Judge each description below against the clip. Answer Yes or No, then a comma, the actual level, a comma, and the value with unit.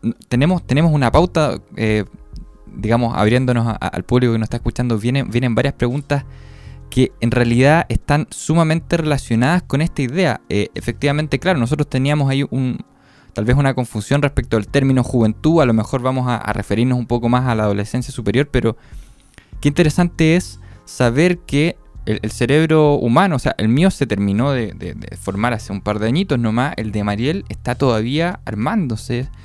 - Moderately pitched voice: No, low, 125 Hz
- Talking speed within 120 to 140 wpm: No, average, 180 wpm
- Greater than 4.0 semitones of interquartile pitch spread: Yes, average, 4.4 semitones